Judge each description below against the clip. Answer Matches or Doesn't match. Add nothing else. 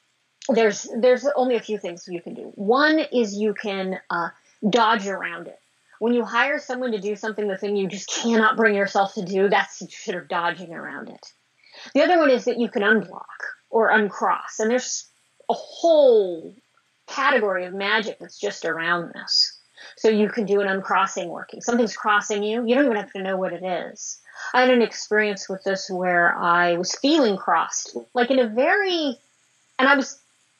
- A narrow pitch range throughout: Doesn't match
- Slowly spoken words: Doesn't match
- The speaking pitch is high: Matches